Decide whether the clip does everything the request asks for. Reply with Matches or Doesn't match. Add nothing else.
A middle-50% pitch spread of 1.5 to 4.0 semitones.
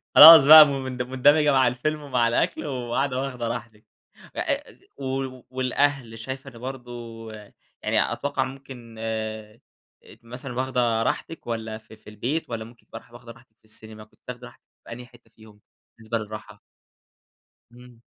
Matches